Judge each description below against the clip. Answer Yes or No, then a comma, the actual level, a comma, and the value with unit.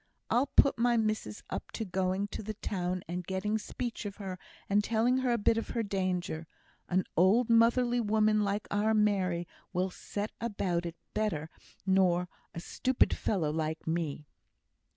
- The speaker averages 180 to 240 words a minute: No, average, 165 wpm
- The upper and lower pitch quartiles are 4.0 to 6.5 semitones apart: No, average, 3.6 semitones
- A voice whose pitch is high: Yes, high, 200 Hz